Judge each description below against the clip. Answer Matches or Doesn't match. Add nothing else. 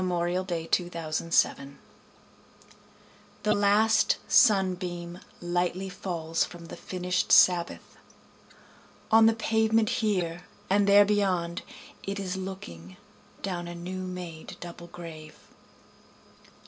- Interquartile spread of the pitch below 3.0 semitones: Matches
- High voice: Doesn't match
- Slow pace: Matches